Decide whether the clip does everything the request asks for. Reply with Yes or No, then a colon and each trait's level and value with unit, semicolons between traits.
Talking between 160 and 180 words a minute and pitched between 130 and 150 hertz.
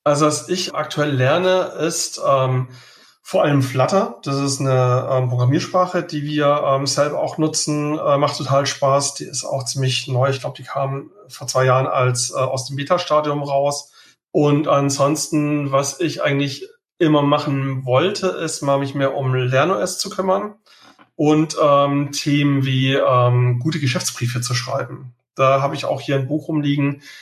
Yes: average, 170 wpm; medium, 140 Hz